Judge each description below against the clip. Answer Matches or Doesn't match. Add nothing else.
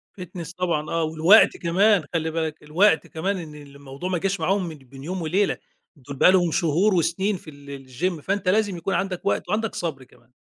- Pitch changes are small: Doesn't match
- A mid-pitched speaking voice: Matches